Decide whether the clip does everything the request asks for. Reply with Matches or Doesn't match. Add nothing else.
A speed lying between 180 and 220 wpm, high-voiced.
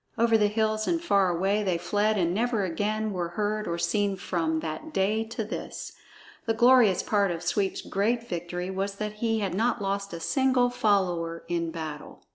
Matches